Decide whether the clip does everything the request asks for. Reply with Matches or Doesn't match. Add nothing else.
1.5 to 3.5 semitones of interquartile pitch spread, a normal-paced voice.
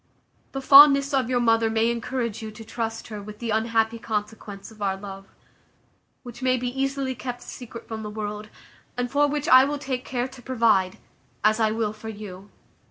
Matches